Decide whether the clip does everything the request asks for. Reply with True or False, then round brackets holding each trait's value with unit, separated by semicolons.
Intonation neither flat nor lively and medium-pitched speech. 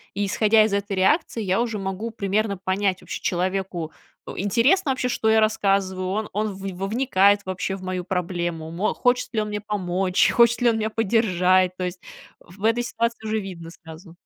False (3.0 semitones; 195 Hz)